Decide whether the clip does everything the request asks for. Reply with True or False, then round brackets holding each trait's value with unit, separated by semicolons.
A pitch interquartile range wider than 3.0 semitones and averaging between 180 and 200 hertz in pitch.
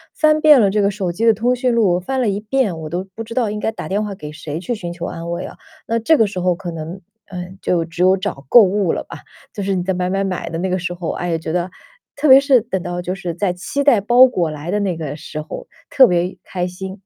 True (4.1 semitones; 190 Hz)